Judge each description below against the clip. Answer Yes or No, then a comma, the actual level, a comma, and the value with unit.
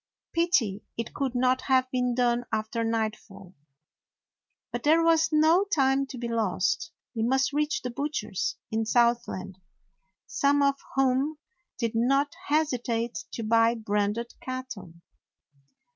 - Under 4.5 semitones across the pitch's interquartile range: Yes, average, 3.7 semitones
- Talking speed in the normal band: No, slow, 130 wpm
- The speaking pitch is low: No, high, 245 Hz